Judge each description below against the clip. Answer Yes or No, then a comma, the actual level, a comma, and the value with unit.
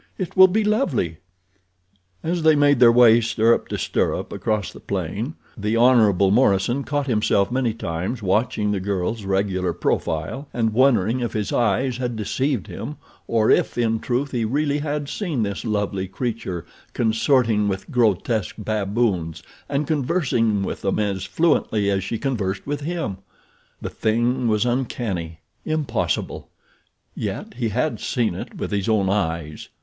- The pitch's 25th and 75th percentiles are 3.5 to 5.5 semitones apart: Yes, average, 4.7 semitones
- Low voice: Yes, low, 115 Hz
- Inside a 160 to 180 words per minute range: No, average, 150 wpm